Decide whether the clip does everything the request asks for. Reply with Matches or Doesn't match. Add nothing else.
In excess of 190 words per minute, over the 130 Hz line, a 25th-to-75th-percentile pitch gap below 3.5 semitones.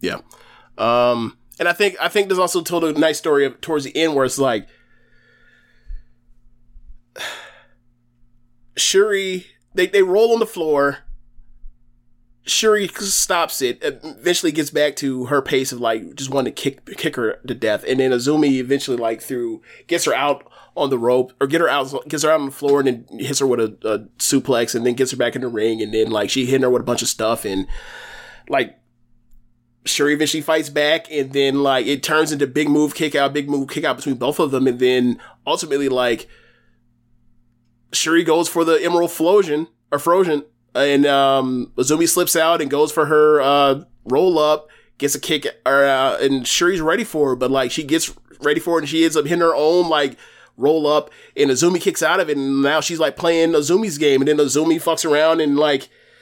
Doesn't match